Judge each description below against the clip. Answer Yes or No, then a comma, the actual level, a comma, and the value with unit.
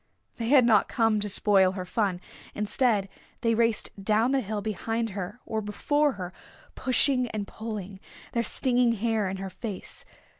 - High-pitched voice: Yes, high, 215 Hz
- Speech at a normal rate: Yes, average, 160 wpm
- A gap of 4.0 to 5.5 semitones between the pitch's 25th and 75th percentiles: No, average, 2.8 semitones